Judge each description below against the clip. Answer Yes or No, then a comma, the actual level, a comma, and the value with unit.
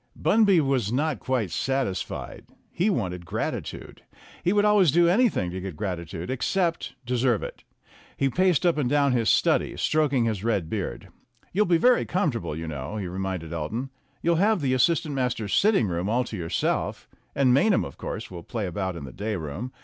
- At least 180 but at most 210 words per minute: Yes, average, 190 wpm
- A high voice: No, low, 125 Hz